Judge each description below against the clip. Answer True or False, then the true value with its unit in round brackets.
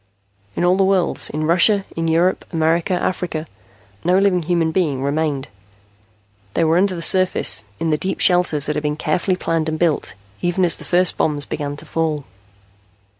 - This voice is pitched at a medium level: True (165 Hz)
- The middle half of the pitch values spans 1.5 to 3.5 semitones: True (2.9 semitones)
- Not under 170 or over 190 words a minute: True (175 wpm)